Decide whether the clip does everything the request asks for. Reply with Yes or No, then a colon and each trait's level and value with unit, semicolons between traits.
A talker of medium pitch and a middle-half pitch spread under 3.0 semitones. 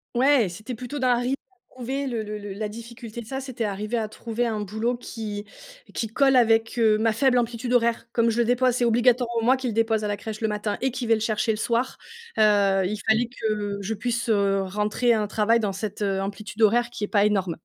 No: high, 225 Hz; narrow, 2.4 semitones